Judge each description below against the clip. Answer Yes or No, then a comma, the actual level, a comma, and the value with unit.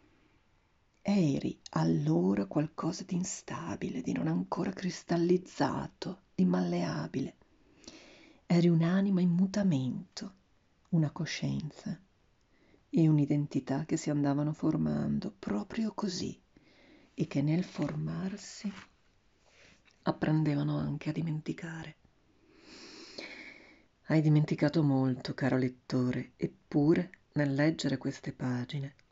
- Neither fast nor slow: No, slow, 90 wpm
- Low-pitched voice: No, medium, 155 Hz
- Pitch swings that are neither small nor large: No, wide, 5.8 semitones